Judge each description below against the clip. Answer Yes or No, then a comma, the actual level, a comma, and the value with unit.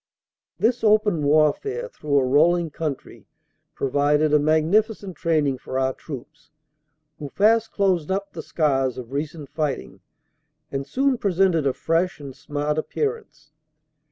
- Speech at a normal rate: No, slow, 130 wpm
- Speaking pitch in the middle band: Yes, medium, 155 Hz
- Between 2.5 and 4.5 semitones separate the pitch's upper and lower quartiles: No, wide, 5.5 semitones